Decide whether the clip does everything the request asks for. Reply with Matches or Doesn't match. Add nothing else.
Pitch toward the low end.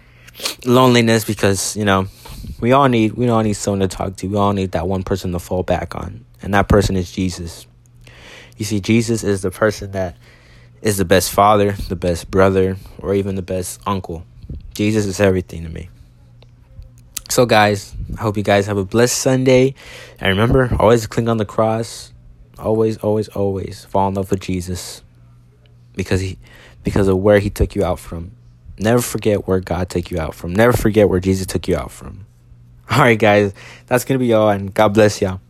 Matches